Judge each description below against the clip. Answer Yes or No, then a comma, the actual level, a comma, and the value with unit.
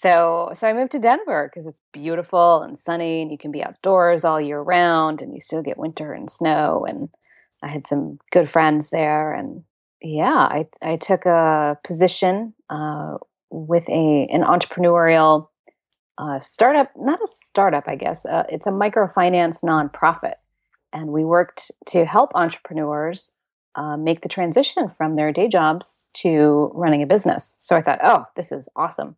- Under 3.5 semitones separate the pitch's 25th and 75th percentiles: Yes, average, 2.8 semitones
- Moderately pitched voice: Yes, medium, 165 Hz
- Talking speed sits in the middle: Yes, average, 170 wpm